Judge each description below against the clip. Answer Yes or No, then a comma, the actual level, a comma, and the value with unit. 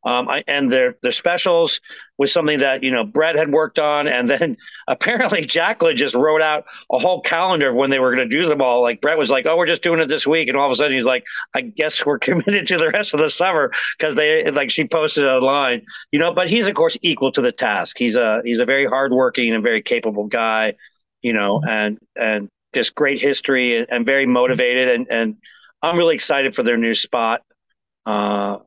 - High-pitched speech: No, medium, 140 Hz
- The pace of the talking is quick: Yes, fast, 225 wpm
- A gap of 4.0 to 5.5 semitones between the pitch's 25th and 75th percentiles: Yes, average, 5.0 semitones